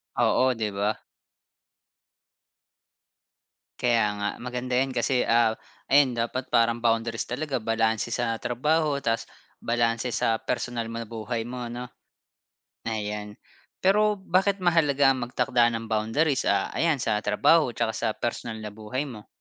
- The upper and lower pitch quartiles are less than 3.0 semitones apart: Yes, narrow, 2.6 semitones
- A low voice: Yes, low, 120 Hz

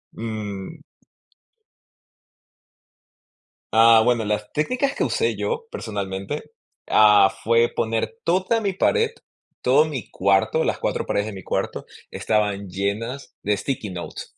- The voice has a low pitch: Yes, low, 110 Hz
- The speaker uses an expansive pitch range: Yes, wide, 6.8 semitones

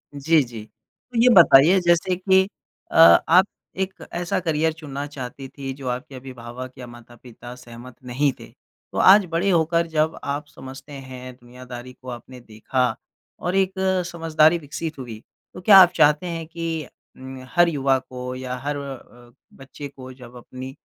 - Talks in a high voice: No, medium, 140 Hz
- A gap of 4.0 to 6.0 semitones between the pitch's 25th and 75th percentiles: Yes, average, 4.7 semitones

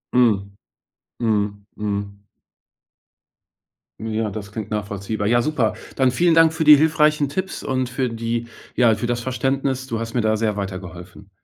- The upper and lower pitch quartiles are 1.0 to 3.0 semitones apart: No, average, 4.3 semitones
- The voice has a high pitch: No, low, 115 Hz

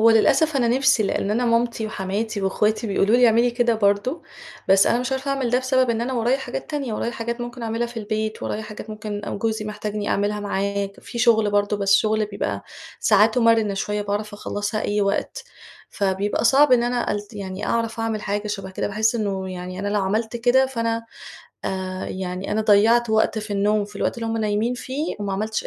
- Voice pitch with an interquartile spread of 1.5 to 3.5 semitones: Yes, narrow, 2.5 semitones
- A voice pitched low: No, high, 215 Hz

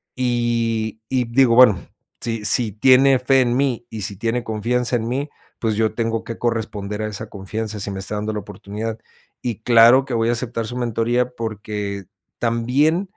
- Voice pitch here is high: No, low, 115 Hz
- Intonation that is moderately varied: No, narrow, 2.3 semitones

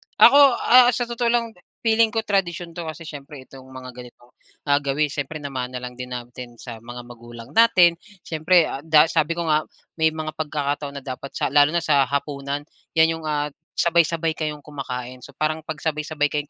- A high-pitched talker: No, medium, 150 Hz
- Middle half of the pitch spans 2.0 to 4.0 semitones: Yes, average, 3.5 semitones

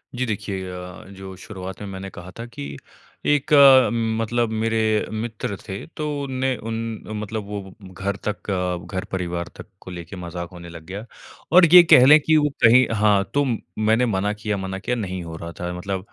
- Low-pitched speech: Yes, low, 100 Hz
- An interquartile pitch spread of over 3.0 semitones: Yes, average, 4.0 semitones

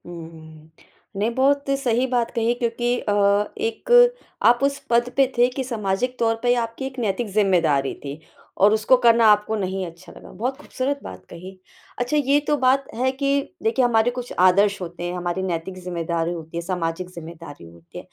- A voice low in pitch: No, high, 220 Hz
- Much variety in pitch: Yes, wide, 6.5 semitones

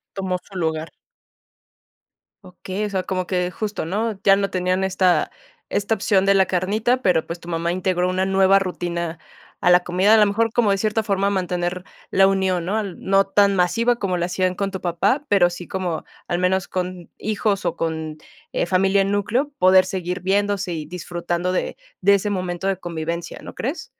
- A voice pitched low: No, medium, 185 Hz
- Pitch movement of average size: No, narrow, 2.0 semitones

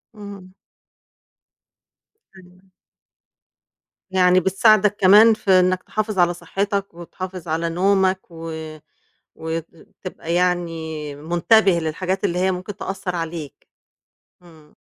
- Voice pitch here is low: No, medium, 180 Hz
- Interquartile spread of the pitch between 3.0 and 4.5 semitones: No, narrow, 2.6 semitones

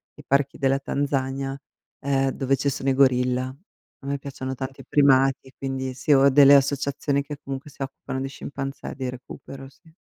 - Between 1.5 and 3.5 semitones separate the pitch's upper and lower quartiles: No, narrow, 0.9 semitones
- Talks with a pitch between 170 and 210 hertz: No, low, 135 Hz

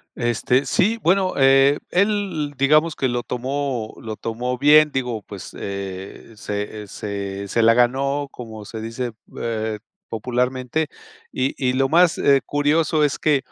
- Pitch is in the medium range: No, low, 130 Hz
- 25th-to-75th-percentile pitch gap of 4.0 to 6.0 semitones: Yes, average, 4.4 semitones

